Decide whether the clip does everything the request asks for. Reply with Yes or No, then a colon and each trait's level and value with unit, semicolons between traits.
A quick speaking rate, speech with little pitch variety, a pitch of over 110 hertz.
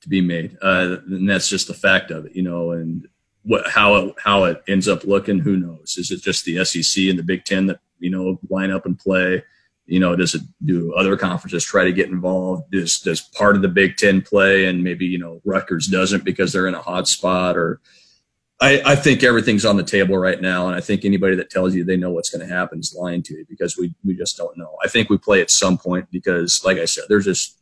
No: fast, 255 wpm; narrow, 1.3 semitones; very low, 95 Hz